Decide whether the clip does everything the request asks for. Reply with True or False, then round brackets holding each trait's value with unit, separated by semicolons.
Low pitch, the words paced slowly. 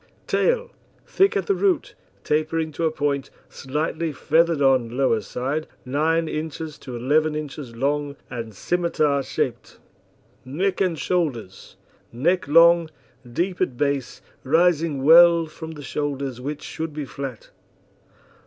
False (150 Hz; 130 wpm)